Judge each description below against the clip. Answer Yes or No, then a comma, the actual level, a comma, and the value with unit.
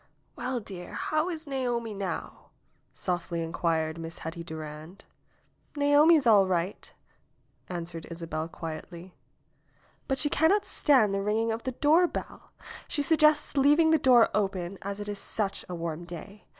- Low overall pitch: No, high, 200 Hz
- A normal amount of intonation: No, wide, 8.2 semitones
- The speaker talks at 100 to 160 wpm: Yes, average, 150 wpm